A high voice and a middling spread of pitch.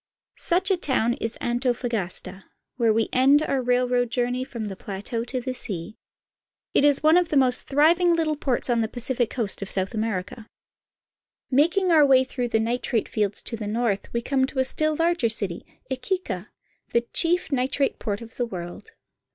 Yes: high, 245 Hz; average, 3.9 semitones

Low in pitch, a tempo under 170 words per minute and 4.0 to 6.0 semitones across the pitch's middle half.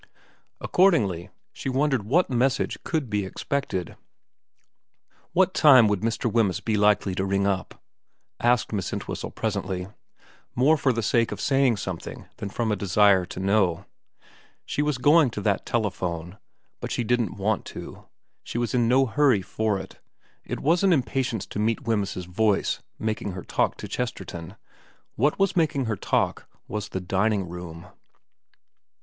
Yes: low, 110 Hz; average, 155 wpm; average, 5.1 semitones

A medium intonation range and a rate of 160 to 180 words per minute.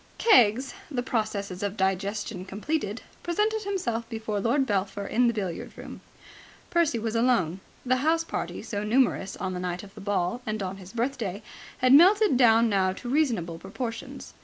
Yes: average, 4.6 semitones; average, 165 wpm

